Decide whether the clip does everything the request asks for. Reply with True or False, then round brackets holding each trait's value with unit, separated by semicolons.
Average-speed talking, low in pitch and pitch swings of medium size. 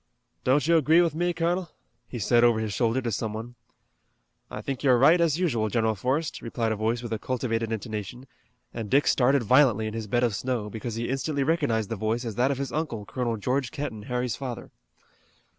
False (210 wpm; 120 Hz; 3.8 semitones)